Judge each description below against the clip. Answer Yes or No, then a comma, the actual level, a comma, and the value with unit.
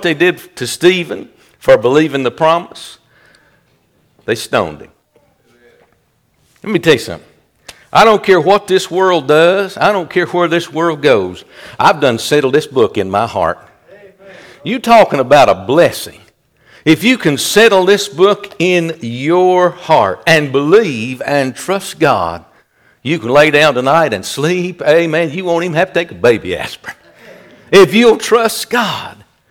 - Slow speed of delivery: No, average, 160 wpm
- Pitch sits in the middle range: Yes, medium, 175 Hz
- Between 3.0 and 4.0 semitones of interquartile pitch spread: Yes, average, 3.7 semitones